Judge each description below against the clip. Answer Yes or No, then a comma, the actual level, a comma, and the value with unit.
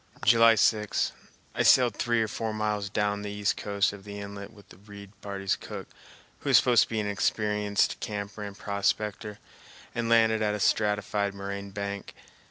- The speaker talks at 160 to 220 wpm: Yes, average, 175 wpm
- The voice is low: Yes, low, 105 Hz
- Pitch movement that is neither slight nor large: No, narrow, 1.1 semitones